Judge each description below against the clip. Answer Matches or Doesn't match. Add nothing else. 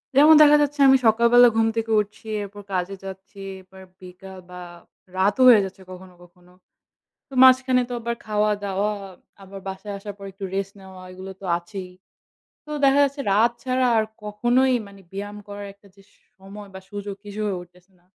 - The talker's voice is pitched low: Doesn't match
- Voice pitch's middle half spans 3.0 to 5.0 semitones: Matches